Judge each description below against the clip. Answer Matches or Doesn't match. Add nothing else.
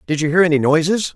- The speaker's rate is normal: Doesn't match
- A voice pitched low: Doesn't match